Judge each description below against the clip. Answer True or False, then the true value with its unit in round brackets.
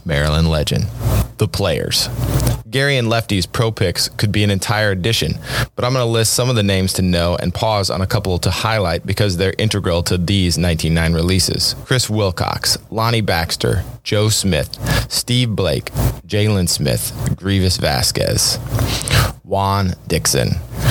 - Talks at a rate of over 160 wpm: False (150 wpm)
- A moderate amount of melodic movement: True (3.9 semitones)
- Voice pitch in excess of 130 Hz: False (105 Hz)